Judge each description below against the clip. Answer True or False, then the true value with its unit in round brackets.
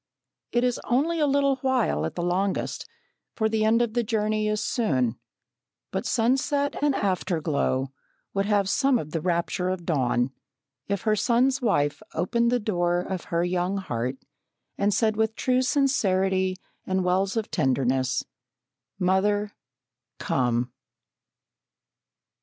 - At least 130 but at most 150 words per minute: True (135 wpm)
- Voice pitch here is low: False (200 Hz)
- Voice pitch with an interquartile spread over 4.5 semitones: True (5.2 semitones)